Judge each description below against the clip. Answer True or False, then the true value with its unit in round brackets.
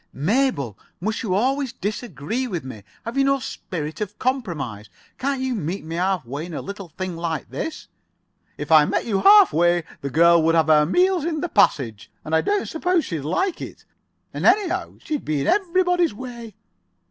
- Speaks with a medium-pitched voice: False (200 Hz)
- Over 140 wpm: True (190 wpm)